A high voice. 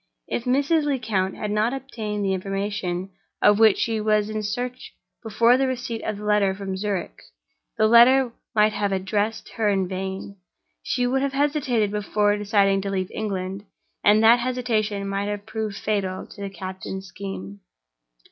Yes: high, 210 Hz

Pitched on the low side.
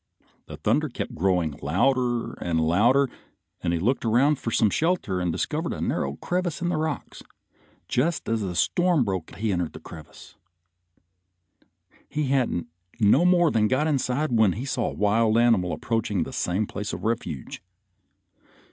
Yes: low, 115 Hz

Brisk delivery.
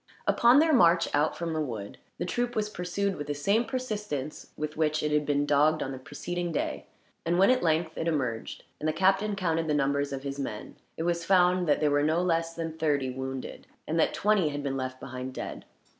Yes: fast, 220 wpm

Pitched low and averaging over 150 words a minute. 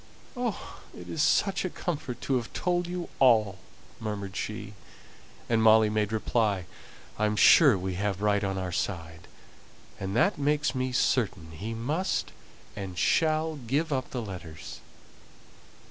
No: low, 110 Hz; average, 145 wpm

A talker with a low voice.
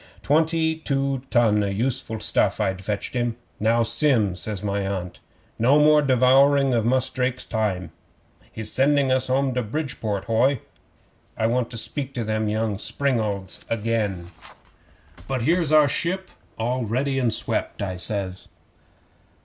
Yes: low, 120 Hz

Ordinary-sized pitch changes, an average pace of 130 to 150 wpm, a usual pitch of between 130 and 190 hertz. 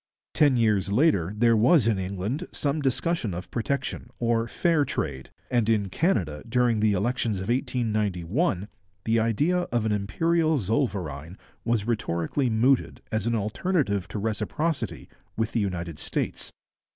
No: average, 4.7 semitones; average, 140 wpm; low, 110 Hz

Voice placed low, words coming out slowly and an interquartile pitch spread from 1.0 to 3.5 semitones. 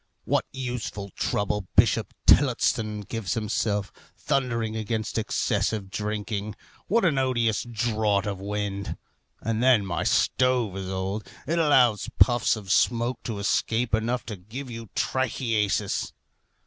Yes: low, 110 Hz; slow, 125 wpm; average, 2.9 semitones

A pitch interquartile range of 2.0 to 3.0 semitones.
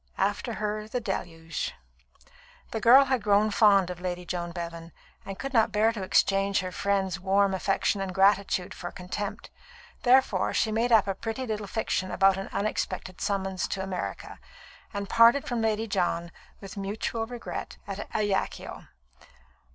Yes: narrow, 2.6 semitones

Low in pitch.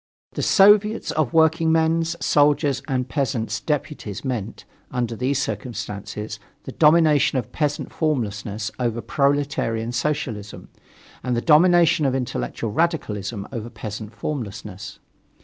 Yes: low, 130 Hz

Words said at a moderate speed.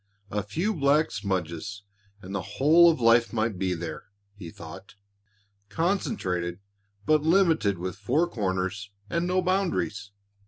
No: slow, 130 wpm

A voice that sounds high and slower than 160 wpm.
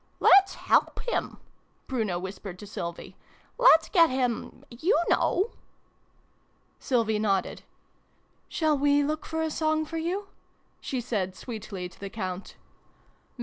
Yes: very high, 255 Hz; average, 150 wpm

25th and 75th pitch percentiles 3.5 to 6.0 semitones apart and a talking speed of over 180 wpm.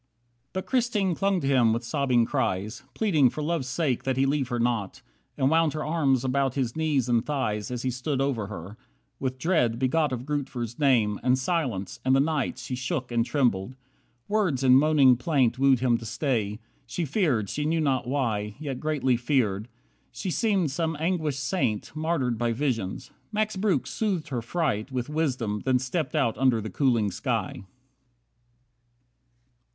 No: average, 4.5 semitones; average, 175 wpm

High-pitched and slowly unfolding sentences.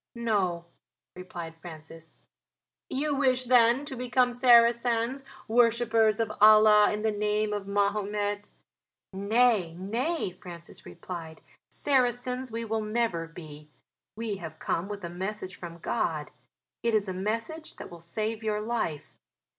Yes: high, 215 Hz; slow, 130 wpm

